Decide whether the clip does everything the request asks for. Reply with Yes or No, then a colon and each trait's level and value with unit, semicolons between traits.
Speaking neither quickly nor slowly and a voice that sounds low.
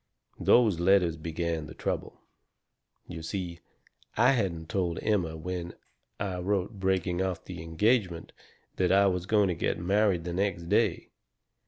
Yes: average, 145 wpm; very low, 90 Hz